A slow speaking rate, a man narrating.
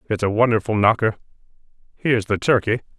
Yes: slow, 120 wpm; male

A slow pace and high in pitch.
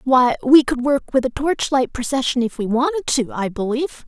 No: fast, 205 wpm; very high, 260 Hz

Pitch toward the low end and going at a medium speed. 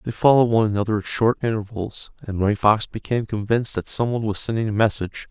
No: low, 110 Hz; fast, 215 wpm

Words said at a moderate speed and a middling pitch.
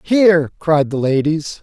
Yes: average, 145 wpm; medium, 160 Hz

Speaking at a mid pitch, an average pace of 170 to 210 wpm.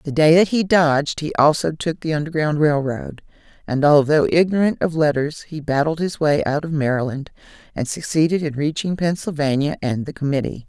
Yes: medium, 150 Hz; average, 180 wpm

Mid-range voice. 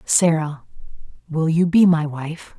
Yes: medium, 160 Hz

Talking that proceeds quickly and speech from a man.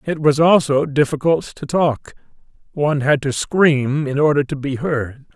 No: average, 170 wpm; male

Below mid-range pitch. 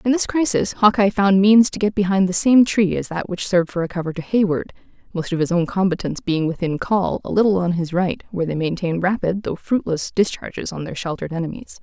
No: medium, 185 Hz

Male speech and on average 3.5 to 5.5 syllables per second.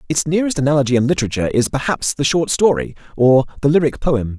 No: male; 6.8 syllables/s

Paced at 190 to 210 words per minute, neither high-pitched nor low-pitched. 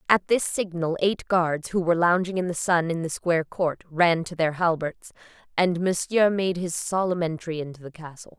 Yes: average, 200 wpm; medium, 170 Hz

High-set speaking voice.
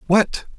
Yes: high, 195 Hz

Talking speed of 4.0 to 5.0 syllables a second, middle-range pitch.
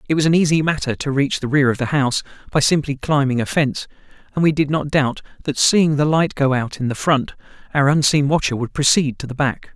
No: 5.9 syllables/s; medium, 145 Hz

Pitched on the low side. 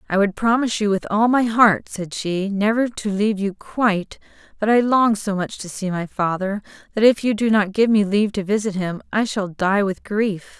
No: high, 205 Hz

